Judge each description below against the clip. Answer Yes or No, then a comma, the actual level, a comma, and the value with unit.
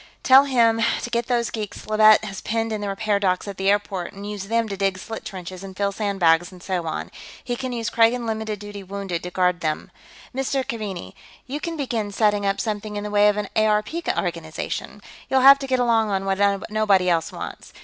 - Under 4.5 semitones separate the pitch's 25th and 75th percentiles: Yes, average, 2.8 semitones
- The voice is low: No, high, 205 Hz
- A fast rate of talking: Yes, fast, 210 wpm